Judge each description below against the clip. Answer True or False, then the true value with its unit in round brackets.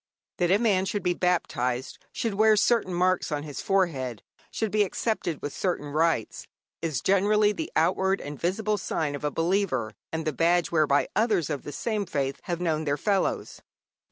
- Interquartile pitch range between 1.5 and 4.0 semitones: False (5.1 semitones)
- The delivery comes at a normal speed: True (180 wpm)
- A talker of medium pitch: True (175 Hz)